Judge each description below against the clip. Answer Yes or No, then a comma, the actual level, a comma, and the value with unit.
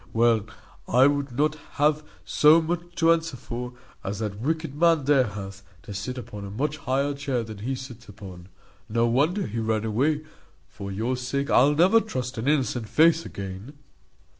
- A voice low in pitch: Yes, low, 130 Hz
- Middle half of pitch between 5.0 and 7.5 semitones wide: Yes, average, 5.3 semitones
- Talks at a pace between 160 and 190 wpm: Yes, average, 175 wpm